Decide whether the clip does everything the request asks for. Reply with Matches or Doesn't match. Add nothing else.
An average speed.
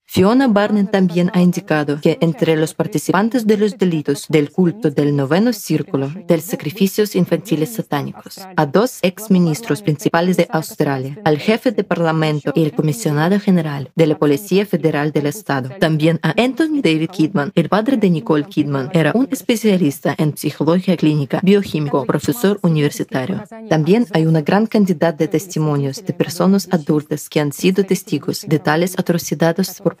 Matches